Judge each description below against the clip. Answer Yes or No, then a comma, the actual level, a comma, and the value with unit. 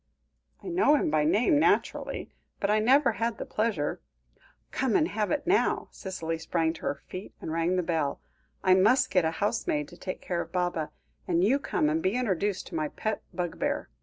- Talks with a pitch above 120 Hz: Yes, medium, 185 Hz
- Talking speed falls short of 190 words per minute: No, average, 200 wpm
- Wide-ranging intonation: Yes, wide, 6.0 semitones